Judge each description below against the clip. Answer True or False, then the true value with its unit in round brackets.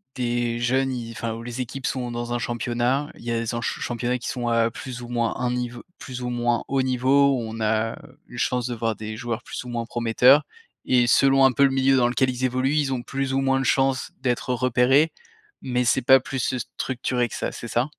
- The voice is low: True (125 Hz)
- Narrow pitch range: True (1.8 semitones)